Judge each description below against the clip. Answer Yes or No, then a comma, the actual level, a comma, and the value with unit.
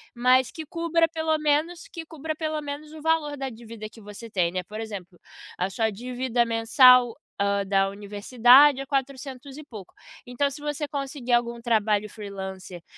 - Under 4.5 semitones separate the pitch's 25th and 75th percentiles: No, wide, 5.6 semitones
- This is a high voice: Yes, very high, 250 Hz